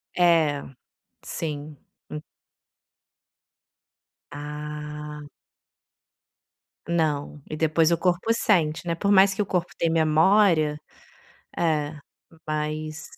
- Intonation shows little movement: Yes, narrow, 2.3 semitones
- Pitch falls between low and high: Yes, medium, 155 Hz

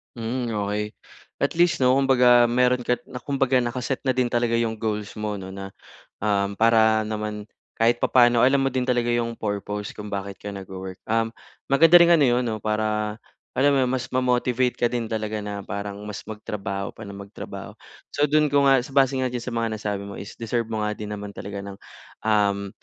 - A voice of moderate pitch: No, low, 115 Hz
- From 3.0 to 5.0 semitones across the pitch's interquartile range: Yes, average, 3.4 semitones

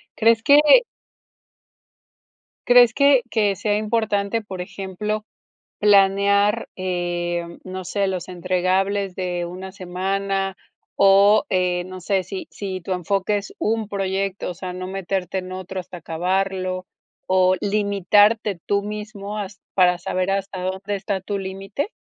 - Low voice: No, high, 195 Hz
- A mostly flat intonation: Yes, narrow, 1.8 semitones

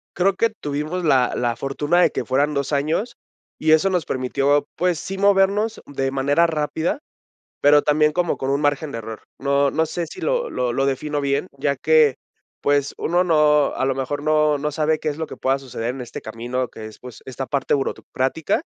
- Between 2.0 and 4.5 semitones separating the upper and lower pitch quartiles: Yes, average, 3.0 semitones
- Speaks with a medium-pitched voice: Yes, medium, 145 Hz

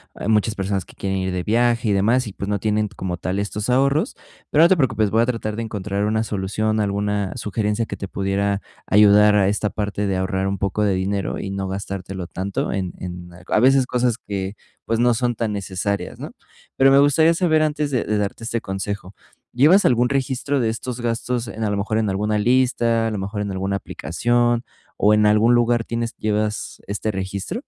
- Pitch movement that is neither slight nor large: Yes, average, 3.3 semitones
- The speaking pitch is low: Yes, low, 105 Hz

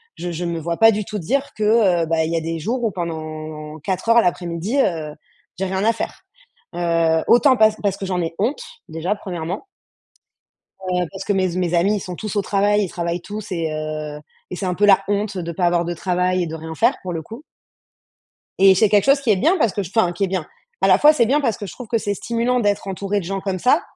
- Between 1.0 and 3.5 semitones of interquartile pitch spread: No, average, 3.9 semitones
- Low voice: No, high, 190 Hz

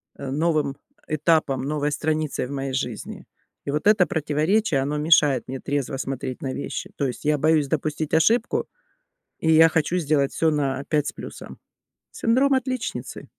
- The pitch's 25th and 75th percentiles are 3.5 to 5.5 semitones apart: No, average, 2.7 semitones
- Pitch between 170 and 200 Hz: No, medium, 150 Hz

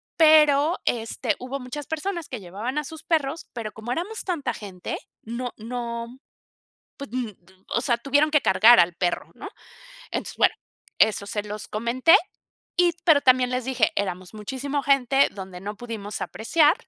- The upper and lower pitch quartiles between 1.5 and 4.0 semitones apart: No, average, 5.2 semitones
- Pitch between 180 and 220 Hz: No, very high, 250 Hz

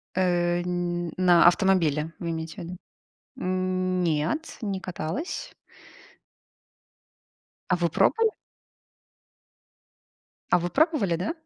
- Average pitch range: No, narrow, 1.9 semitones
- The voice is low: No, medium, 180 Hz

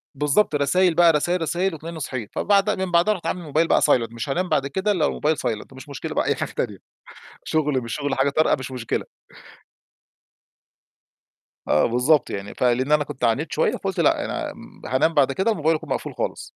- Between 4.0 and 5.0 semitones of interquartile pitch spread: Yes, average, 4.6 semitones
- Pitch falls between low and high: Yes, medium, 150 Hz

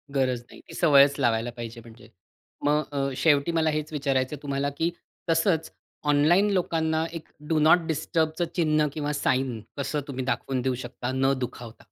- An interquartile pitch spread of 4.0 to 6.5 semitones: No, average, 3.4 semitones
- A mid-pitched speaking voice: Yes, medium, 145 Hz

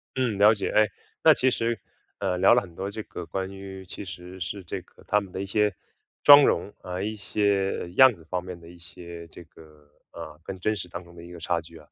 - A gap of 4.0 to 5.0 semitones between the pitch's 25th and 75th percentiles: No, average, 3.1 semitones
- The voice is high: No, very low, 95 Hz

